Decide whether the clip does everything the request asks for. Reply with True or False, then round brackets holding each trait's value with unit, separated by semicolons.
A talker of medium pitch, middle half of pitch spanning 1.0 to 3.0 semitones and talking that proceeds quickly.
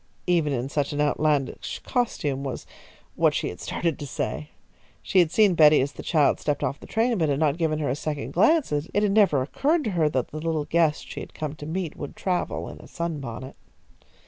False (155 Hz; 3.5 semitones; 220 wpm)